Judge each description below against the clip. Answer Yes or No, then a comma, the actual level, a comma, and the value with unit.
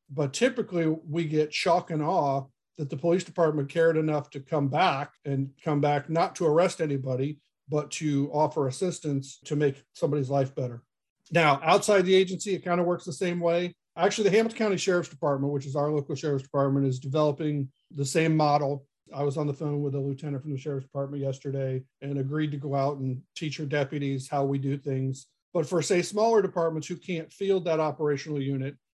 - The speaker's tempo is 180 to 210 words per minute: Yes, average, 200 wpm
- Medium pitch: Yes, medium, 150 Hz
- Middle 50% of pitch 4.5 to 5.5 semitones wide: No, average, 3.2 semitones